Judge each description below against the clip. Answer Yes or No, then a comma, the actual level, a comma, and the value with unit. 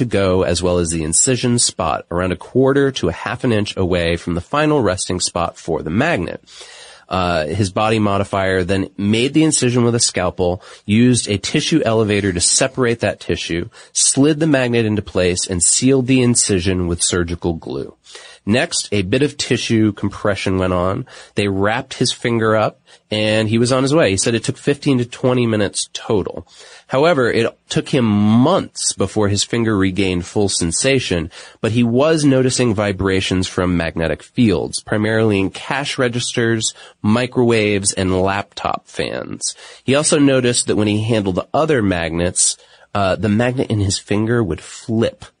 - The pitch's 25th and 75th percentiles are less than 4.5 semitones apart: No, average, 4.8 semitones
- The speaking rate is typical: Yes, average, 170 wpm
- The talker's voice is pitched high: No, low, 105 Hz